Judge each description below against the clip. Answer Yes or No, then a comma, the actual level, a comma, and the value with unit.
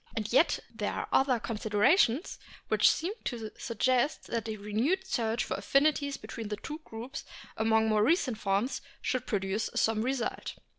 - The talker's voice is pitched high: Yes, high, 230 Hz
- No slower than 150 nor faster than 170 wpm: Yes, average, 155 wpm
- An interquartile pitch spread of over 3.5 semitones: Yes, average, 3.9 semitones